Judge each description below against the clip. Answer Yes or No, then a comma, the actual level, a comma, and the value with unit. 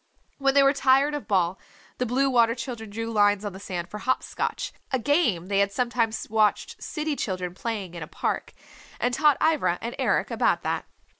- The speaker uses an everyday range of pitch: Yes, average, 5.0 semitones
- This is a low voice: No, high, 230 Hz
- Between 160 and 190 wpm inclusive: No, average, 200 wpm